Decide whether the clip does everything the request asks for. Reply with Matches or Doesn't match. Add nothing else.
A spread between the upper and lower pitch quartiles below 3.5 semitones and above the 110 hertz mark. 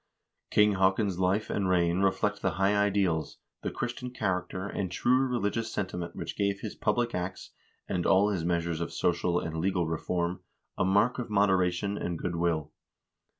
Doesn't match